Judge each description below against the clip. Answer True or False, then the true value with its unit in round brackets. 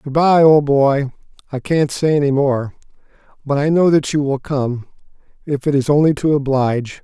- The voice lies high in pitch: False (140 Hz)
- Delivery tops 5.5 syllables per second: False (4.9 syllables/s)